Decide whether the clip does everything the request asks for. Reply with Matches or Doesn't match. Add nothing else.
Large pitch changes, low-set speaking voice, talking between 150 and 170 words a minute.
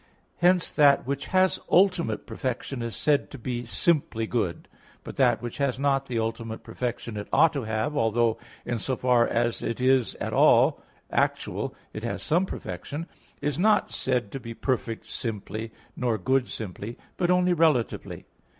Doesn't match